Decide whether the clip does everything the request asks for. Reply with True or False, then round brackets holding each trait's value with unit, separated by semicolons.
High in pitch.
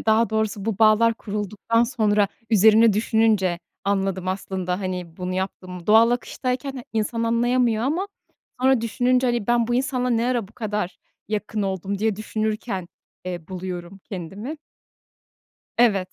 True (215 Hz)